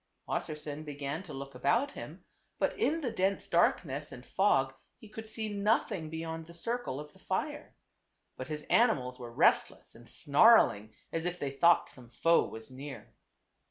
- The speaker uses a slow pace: No, average, 165 wpm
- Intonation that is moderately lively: No, wide, 6.5 semitones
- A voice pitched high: No, medium, 155 Hz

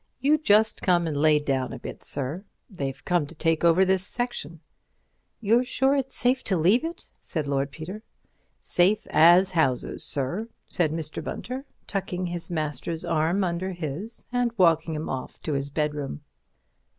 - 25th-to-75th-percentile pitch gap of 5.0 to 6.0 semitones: Yes, wide, 5.4 semitones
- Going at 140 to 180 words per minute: Yes, average, 160 wpm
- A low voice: No, medium, 170 Hz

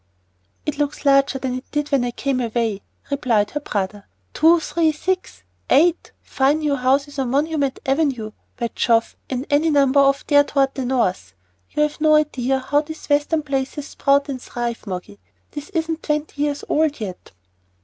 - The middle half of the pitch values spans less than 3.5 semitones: Yes, average, 3.0 semitones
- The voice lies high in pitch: Yes, very high, 280 Hz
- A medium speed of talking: Yes, average, 170 wpm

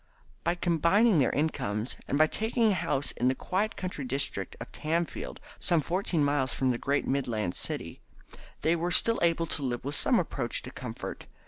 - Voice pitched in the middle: Yes, medium, 155 Hz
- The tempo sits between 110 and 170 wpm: No, average, 185 wpm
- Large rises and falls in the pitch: No, average, 4.8 semitones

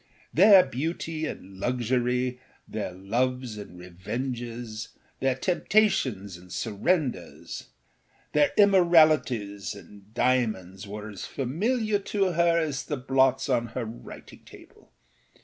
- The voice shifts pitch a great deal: Yes, wide, 6.8 semitones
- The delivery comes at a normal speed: No, slow, 110 wpm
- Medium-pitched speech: No, low, 125 Hz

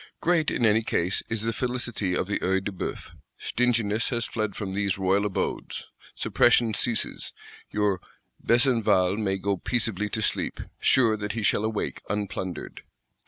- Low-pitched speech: Yes, low, 105 Hz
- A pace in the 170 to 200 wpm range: No, average, 155 wpm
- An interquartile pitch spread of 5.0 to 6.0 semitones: No, average, 2.9 semitones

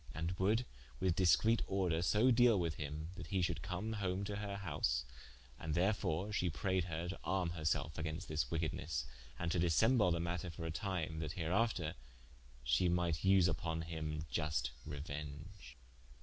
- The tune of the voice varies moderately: Yes, average, 3.5 semitones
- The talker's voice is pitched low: Yes, very low, 85 Hz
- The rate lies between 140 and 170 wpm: Yes, average, 165 wpm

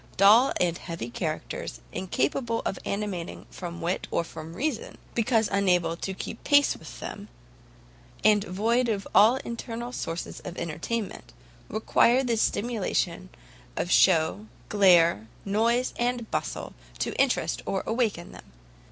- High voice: Yes, high, 200 Hz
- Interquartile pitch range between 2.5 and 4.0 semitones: No, average, 5.1 semitones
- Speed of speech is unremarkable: No, slow, 130 wpm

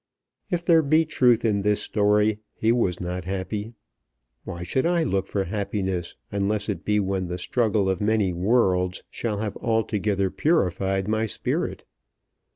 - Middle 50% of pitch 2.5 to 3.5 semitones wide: Yes, average, 2.8 semitones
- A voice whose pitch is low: Yes, low, 105 Hz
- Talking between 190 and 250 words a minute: No, average, 155 wpm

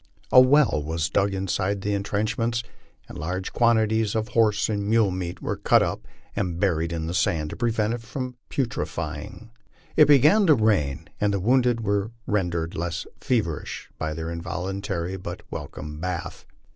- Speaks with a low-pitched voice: Yes, low, 100 Hz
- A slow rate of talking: No, average, 165 wpm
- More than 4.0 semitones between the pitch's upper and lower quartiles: Yes, average, 5.1 semitones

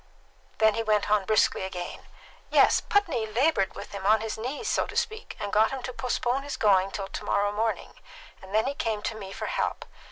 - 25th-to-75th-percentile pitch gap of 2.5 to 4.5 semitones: Yes, average, 3.7 semitones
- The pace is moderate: No, fast, 215 wpm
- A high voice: Yes, high, 220 Hz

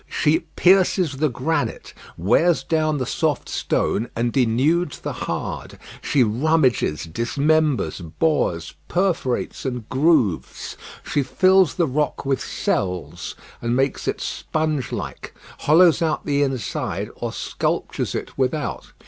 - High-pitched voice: No, medium, 140 Hz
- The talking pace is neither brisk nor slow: No, slow, 125 wpm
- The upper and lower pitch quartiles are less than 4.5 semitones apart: No, average, 4.8 semitones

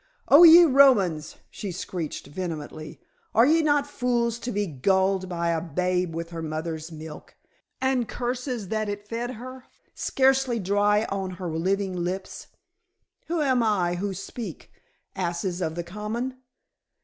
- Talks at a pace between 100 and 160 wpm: Yes, average, 145 wpm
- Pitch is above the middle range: Yes, high, 195 Hz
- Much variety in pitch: Yes, wide, 6.0 semitones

